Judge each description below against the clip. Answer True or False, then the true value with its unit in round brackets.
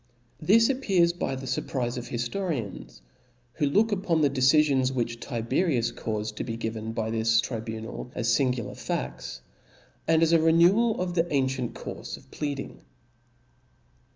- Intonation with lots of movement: True (6.1 semitones)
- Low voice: True (130 Hz)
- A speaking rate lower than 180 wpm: True (145 wpm)